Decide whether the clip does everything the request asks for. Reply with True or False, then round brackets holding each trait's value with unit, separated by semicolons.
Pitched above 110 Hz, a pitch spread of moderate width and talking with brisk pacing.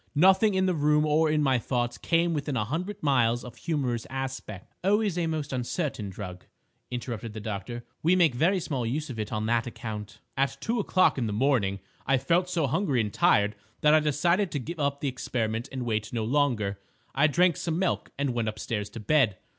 False (135 Hz; 5.8 semitones; 210 wpm)